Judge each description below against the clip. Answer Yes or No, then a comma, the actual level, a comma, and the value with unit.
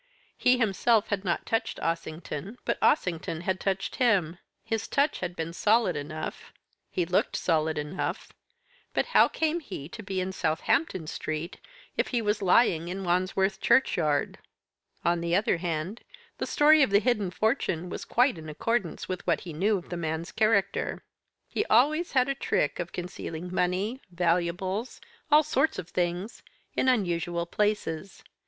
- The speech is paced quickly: No, average, 160 wpm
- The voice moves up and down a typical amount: Yes, average, 4.8 semitones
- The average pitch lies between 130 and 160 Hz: No, medium, 185 Hz